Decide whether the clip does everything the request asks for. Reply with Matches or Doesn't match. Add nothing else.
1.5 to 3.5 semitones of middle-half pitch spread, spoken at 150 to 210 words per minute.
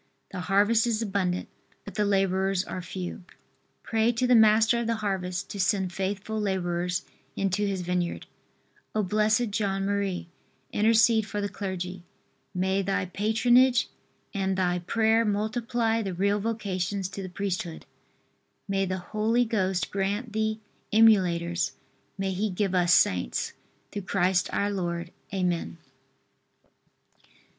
Doesn't match